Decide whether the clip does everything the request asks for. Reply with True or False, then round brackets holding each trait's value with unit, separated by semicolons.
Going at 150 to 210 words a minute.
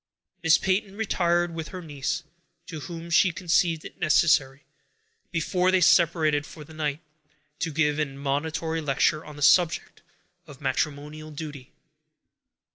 False (135 wpm)